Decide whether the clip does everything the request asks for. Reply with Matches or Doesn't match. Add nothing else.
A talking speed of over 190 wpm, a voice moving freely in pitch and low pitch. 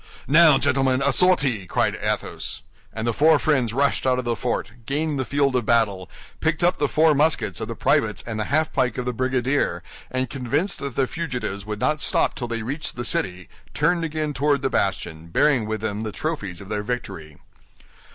Doesn't match